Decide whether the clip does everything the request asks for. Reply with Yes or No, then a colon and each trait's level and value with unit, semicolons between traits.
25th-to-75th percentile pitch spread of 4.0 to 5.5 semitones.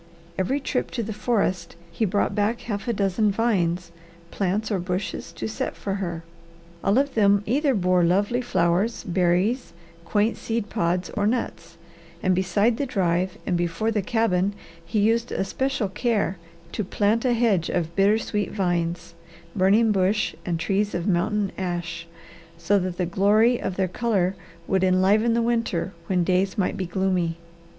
No: average, 3.5 semitones